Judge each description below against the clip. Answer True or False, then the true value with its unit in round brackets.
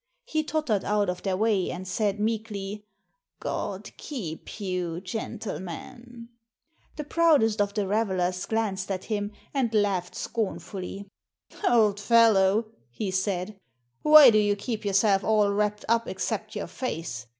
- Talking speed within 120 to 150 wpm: True (140 wpm)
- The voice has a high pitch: True (205 Hz)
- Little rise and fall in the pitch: False (3.0 semitones)